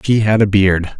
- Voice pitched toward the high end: No, low, 100 Hz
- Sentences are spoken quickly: Yes, fast, 240 wpm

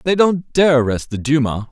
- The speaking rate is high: Yes, fast, 210 wpm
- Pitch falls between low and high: Yes, medium, 145 Hz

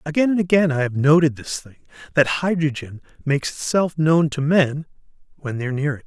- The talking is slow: No, average, 200 wpm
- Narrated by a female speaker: No, male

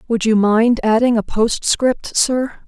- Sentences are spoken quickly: No, average, 155 wpm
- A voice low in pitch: No, high, 230 Hz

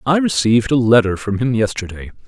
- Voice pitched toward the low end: Yes, low, 120 Hz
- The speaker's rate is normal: Yes, average, 185 wpm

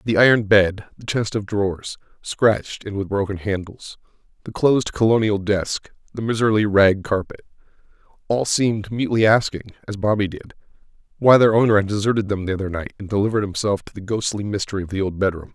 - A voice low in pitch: Yes, low, 105 Hz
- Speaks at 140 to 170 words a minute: No, average, 180 wpm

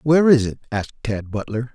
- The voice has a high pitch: No, low, 120 Hz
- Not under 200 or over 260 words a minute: Yes, fast, 205 wpm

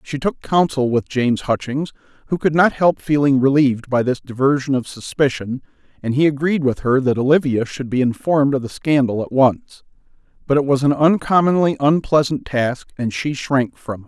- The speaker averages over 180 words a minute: Yes, average, 190 wpm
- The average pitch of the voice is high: No, low, 135 Hz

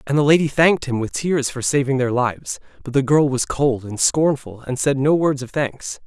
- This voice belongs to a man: Yes, male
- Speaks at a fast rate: Yes, fast, 235 wpm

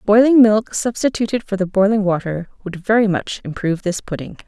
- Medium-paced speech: Yes, average, 175 wpm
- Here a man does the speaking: No, female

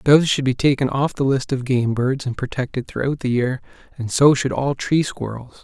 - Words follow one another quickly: Yes, fast, 225 wpm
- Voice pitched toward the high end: No, low, 130 Hz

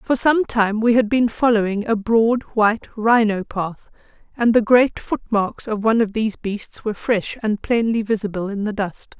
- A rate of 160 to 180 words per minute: No, average, 190 wpm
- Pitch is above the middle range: Yes, high, 220 Hz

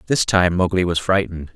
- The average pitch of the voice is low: Yes, very low, 90 Hz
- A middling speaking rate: Yes, average, 195 wpm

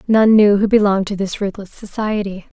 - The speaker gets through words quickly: No, average, 185 wpm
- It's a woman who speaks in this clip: Yes, female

